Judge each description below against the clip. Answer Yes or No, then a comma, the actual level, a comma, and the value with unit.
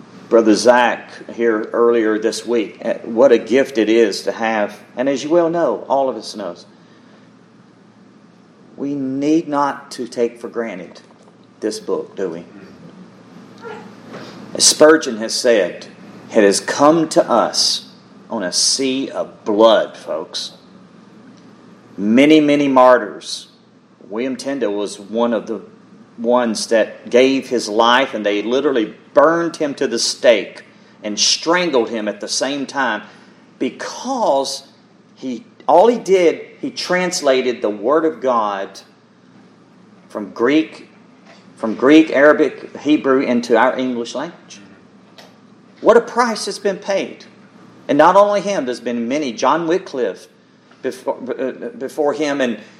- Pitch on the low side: Yes, low, 130 Hz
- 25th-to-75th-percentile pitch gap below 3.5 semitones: No, average, 5.1 semitones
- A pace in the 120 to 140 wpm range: Yes, slow, 135 wpm